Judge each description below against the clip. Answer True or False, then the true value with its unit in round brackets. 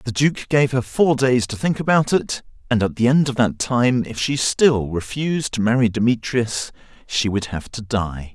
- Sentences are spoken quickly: True (210 wpm)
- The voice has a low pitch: True (120 Hz)